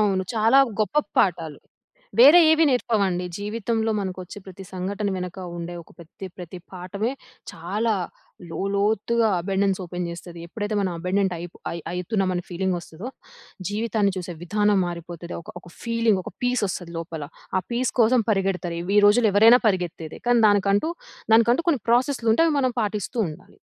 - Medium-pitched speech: No, high, 200 Hz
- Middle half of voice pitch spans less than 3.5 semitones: No, average, 4.1 semitones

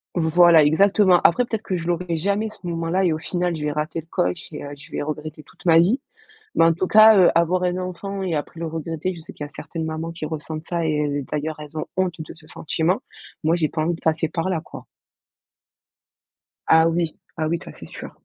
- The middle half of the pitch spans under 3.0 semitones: Yes, narrow, 2.4 semitones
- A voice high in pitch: No, medium, 165 Hz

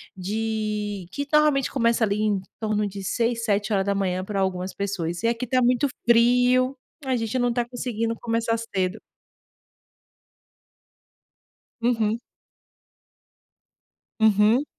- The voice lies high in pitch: Yes, high, 225 Hz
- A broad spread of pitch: No, average, 3.2 semitones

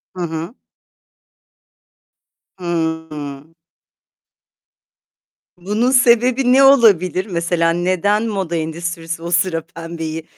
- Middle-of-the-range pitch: Yes, medium, 175 Hz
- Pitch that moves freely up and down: No, average, 4.2 semitones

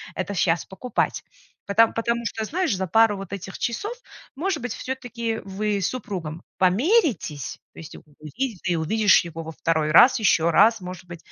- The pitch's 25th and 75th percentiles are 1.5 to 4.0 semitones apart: No, wide, 5.5 semitones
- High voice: Yes, high, 200 Hz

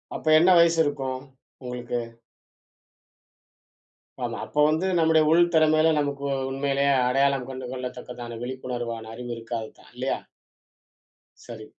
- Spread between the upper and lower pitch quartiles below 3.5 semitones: No, average, 3.8 semitones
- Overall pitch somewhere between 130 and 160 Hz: Yes, low, 135 Hz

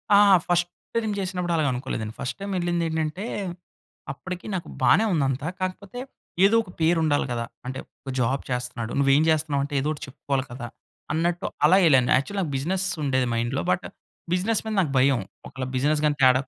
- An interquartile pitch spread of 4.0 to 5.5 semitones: Yes, average, 5.2 semitones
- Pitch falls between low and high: Yes, medium, 150 Hz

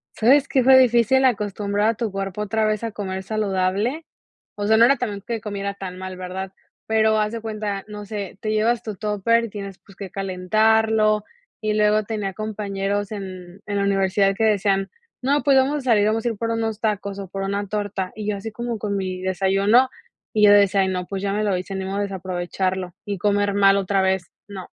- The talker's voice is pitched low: No, high, 205 Hz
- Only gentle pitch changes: Yes, narrow, 2.1 semitones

